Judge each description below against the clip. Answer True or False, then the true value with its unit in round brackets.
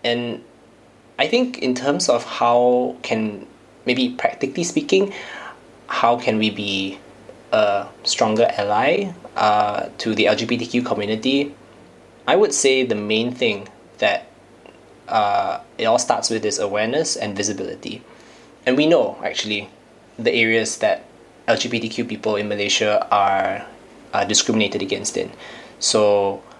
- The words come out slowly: True (125 wpm)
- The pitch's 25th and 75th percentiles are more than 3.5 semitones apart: False (3.1 semitones)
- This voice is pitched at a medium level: False (115 Hz)